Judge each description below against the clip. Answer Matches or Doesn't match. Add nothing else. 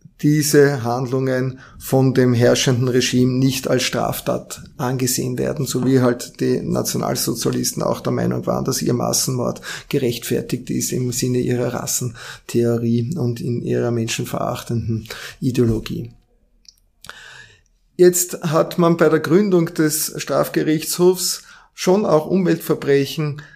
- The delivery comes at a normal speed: Doesn't match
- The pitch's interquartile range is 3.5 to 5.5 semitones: Matches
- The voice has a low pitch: Matches